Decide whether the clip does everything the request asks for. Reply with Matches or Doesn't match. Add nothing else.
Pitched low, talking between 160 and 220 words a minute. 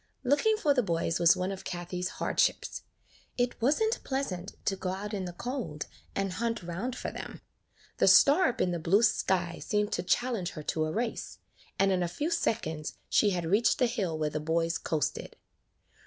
Doesn't match